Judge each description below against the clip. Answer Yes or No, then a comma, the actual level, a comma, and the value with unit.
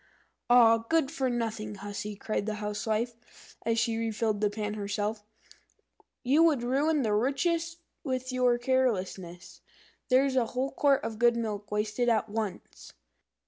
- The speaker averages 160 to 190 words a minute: No, average, 140 wpm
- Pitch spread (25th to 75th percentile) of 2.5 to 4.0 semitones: Yes, average, 3.5 semitones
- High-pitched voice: Yes, high, 230 Hz